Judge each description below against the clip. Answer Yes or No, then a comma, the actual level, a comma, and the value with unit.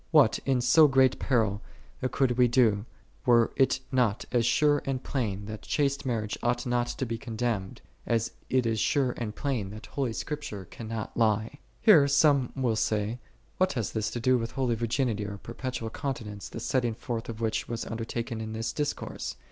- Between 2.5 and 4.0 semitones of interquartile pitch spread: Yes, average, 3.0 semitones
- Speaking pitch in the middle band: No, low, 120 Hz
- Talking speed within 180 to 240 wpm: Yes, average, 195 wpm